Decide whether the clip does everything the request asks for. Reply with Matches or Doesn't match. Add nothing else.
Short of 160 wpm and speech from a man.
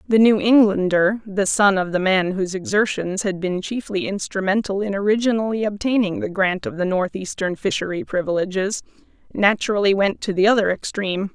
Doesn't match